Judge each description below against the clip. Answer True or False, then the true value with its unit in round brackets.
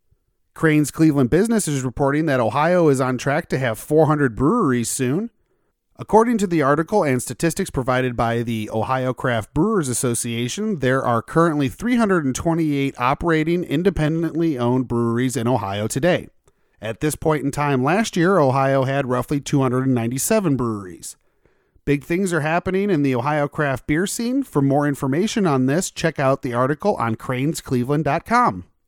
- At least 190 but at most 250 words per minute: False (150 wpm)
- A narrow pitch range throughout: False (4.5 semitones)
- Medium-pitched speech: True (145 Hz)